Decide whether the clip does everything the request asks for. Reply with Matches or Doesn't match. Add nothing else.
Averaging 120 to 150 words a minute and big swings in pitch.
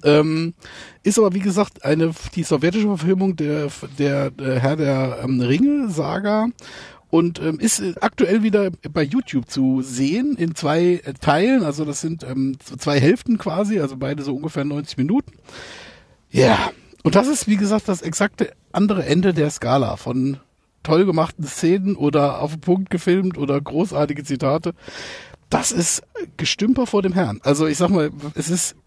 Doesn't match